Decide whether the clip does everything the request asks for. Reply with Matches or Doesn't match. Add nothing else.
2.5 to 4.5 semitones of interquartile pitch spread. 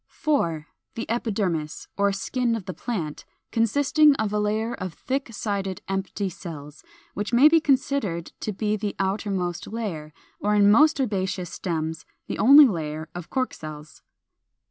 Doesn't match